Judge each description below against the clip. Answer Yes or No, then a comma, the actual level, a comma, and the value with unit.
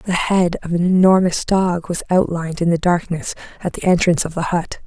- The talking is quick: Yes, fast, 210 wpm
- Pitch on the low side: No, medium, 175 Hz